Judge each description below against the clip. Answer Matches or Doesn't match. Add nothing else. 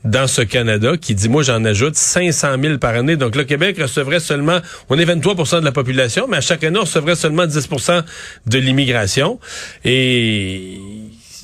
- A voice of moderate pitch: Matches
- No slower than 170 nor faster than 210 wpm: Matches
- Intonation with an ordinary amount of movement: Doesn't match